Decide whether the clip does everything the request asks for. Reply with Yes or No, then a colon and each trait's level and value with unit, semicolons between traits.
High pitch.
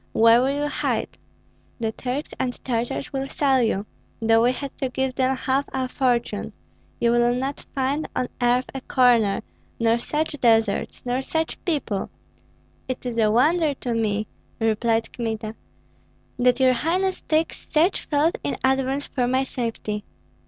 Yes: very high, 250 Hz